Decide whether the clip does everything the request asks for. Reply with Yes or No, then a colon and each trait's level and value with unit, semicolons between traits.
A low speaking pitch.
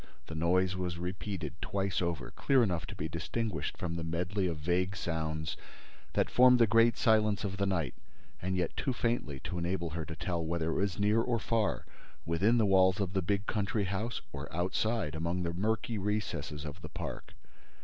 Yes: very low, 95 Hz